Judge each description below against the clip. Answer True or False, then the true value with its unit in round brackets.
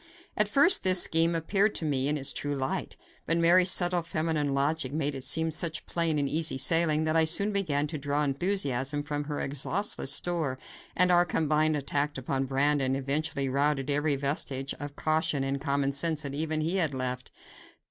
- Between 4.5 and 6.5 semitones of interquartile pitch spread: False (3.0 semitones)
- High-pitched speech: False (150 Hz)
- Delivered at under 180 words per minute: False (185 wpm)